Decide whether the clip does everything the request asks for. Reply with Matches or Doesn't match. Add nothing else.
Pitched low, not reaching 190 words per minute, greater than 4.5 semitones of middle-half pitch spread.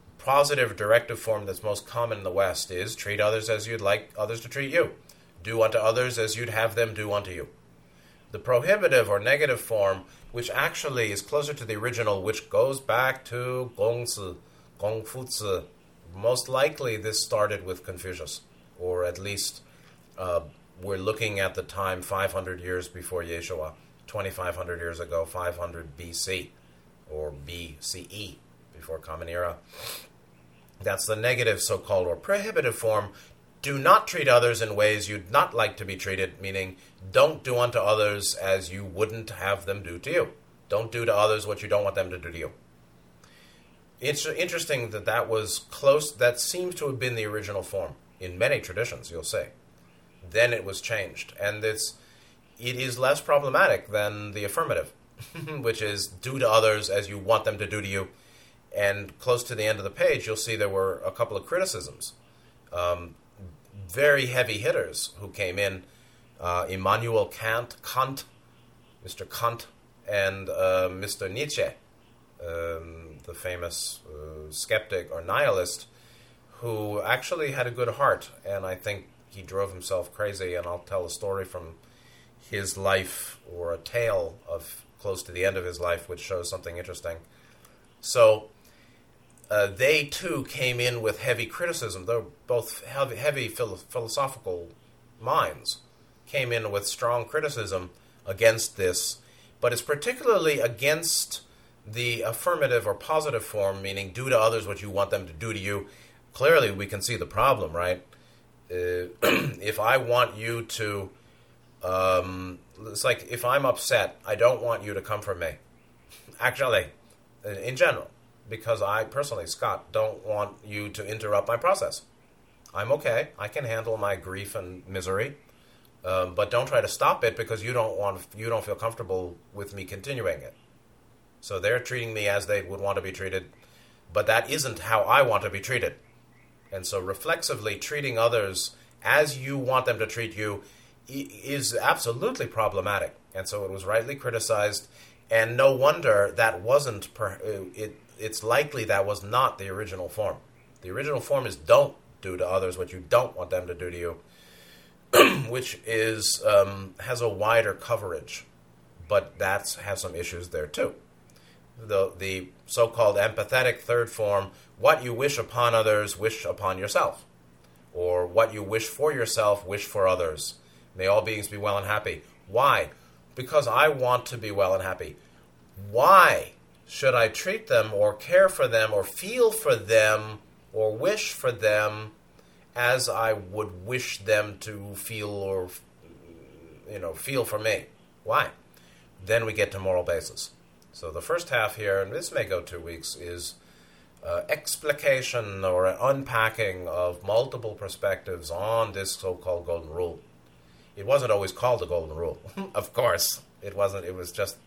Matches